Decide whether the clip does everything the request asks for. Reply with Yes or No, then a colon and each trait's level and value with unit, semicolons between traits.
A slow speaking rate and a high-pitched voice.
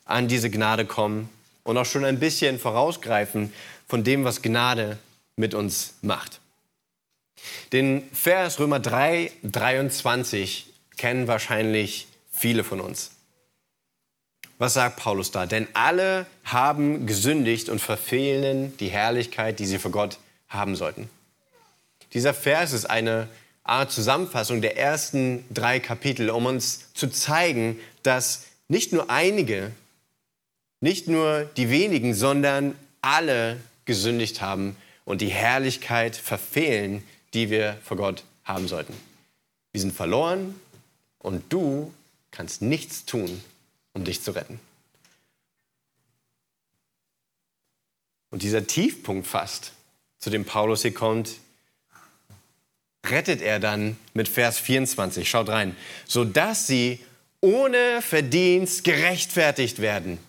No: slow, 115 wpm; low, 120 Hz